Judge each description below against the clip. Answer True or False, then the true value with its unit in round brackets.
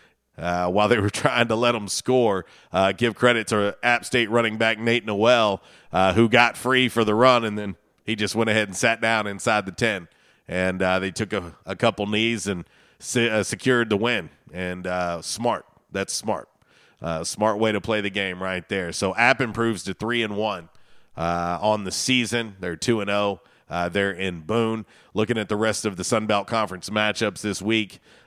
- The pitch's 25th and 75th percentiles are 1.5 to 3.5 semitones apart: True (3.2 semitones)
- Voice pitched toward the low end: True (110 Hz)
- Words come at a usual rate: False (210 wpm)